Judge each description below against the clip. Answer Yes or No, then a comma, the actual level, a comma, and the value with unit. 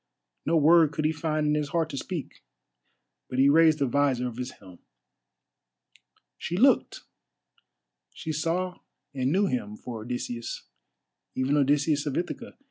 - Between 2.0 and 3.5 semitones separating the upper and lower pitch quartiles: No, average, 4.2 semitones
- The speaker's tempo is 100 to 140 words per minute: Yes, slow, 135 wpm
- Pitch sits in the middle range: Yes, medium, 145 Hz